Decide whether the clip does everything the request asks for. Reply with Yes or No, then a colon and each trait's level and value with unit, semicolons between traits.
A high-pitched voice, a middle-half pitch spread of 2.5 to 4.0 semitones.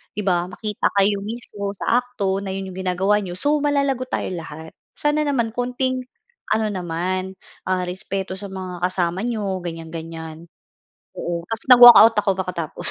No: high, 195 Hz; average, 4.5 semitones